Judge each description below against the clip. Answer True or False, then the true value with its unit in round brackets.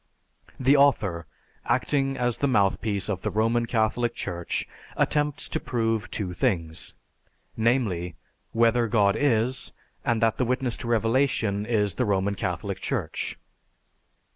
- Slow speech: True (130 wpm)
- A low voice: True (115 Hz)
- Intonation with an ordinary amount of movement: True (3.6 semitones)